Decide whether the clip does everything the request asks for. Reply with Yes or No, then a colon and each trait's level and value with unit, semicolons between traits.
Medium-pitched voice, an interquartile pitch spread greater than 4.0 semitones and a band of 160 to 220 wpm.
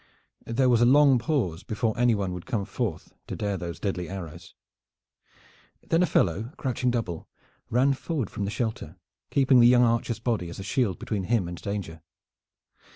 No: low, 110 Hz; average, 4.8 semitones; average, 170 wpm